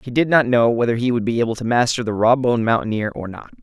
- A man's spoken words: Yes, male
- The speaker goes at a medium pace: No, fast, 280 wpm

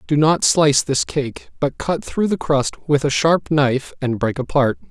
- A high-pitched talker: No, medium, 145 Hz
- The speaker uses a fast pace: Yes, fast, 210 wpm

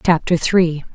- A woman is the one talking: Yes, female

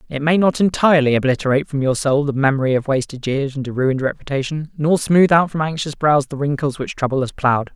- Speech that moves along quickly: Yes, fast, 225 wpm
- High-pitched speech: No, medium, 145 Hz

